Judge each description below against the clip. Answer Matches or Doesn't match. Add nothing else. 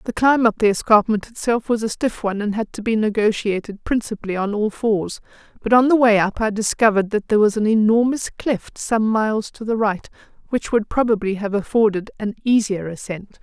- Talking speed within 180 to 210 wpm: Matches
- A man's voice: Doesn't match